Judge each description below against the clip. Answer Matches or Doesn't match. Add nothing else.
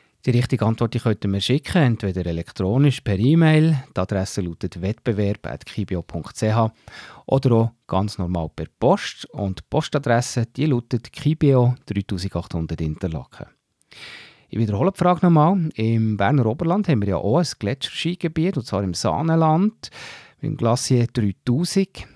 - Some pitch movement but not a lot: Doesn't match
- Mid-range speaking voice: Doesn't match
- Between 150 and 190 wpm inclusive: Doesn't match